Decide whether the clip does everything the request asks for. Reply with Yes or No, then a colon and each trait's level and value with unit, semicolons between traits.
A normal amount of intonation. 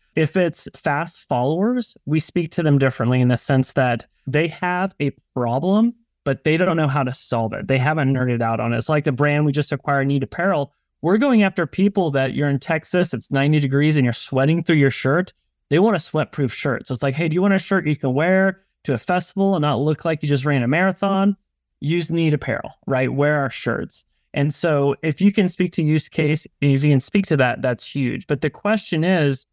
Yes: average, 4.7 semitones